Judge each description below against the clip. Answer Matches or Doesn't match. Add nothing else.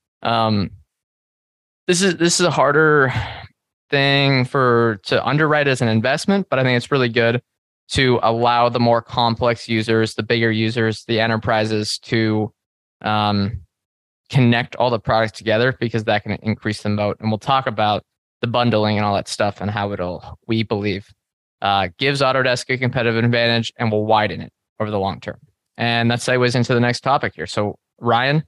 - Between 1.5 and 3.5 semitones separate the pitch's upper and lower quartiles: Matches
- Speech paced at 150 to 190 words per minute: Matches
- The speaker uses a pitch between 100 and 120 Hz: Matches